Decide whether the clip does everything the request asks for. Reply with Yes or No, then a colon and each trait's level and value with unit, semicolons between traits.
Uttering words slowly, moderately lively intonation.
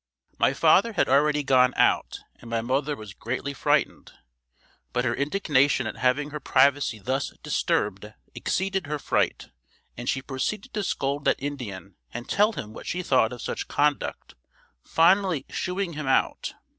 No: average, 155 wpm; average, 3.4 semitones